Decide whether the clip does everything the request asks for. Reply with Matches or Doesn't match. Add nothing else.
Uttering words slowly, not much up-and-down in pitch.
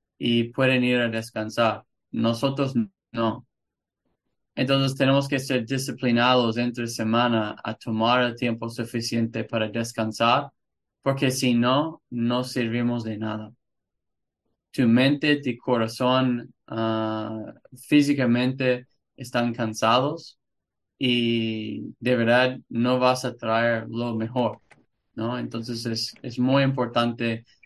Matches